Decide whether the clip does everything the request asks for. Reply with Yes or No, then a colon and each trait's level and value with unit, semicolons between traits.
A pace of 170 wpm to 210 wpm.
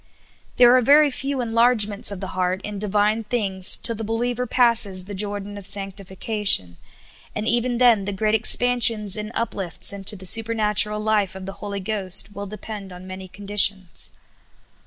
No: average, 160 wpm